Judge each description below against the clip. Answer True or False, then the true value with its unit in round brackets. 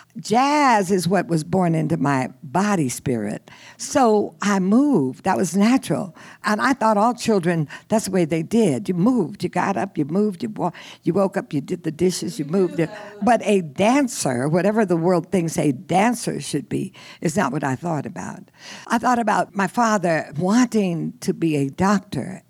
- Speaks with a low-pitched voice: False (190 Hz)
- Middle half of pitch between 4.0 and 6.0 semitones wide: True (4.5 semitones)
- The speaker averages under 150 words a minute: False (180 wpm)